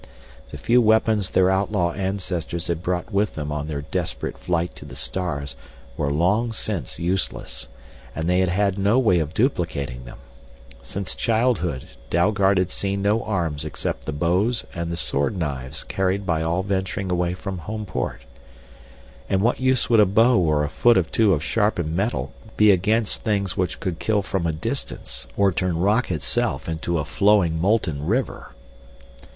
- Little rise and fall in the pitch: No, average, 4.2 semitones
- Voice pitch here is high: No, very low, 90 Hz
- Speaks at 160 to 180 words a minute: Yes, average, 170 wpm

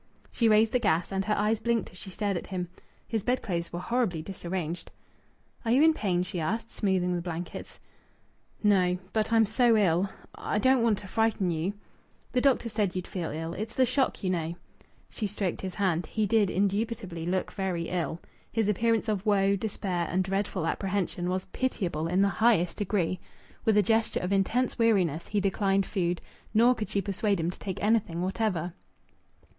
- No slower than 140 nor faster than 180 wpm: No, average, 190 wpm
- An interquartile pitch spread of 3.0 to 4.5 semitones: Yes, average, 3.7 semitones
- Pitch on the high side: Yes, high, 195 Hz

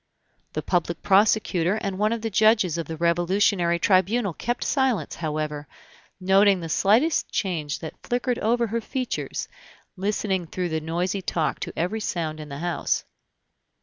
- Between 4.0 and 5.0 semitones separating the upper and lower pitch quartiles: Yes, average, 4.3 semitones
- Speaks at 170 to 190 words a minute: No, average, 150 wpm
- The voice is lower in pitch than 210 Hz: Yes, high, 190 Hz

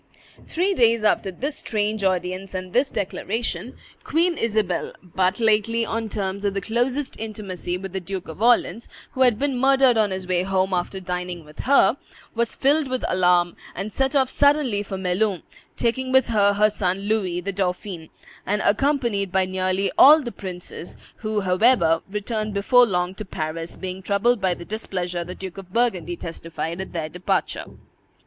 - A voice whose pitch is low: No, high, 200 Hz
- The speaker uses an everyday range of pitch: Yes, average, 4.2 semitones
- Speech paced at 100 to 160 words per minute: No, average, 170 wpm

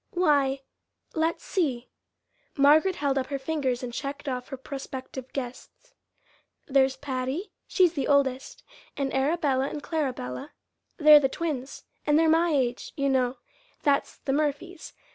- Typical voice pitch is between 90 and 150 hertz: No, very high, 280 Hz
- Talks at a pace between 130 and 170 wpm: Yes, average, 140 wpm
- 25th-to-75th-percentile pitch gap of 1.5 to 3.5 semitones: Yes, narrow, 2.6 semitones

